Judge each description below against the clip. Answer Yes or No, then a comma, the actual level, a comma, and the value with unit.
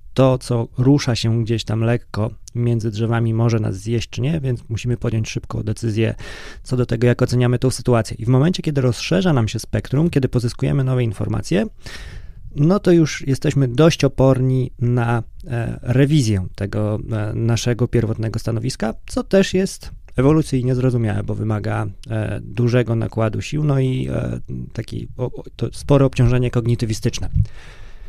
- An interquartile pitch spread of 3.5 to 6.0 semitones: No, average, 2.9 semitones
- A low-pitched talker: Yes, low, 120 Hz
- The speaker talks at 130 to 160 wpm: Yes, average, 140 wpm